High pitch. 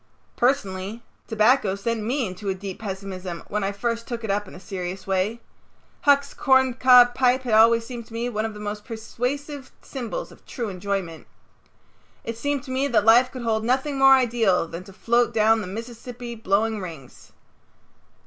Yes: high, 225 Hz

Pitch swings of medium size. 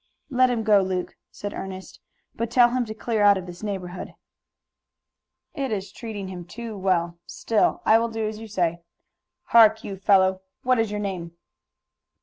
Yes: average, 3.2 semitones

